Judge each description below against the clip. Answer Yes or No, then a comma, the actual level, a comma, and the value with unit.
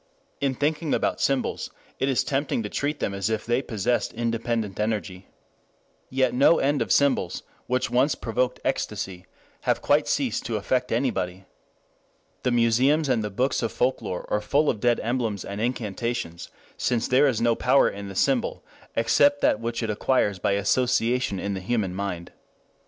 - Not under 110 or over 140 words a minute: No, average, 170 wpm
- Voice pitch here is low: Yes, low, 120 Hz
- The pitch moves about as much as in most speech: Yes, average, 4.1 semitones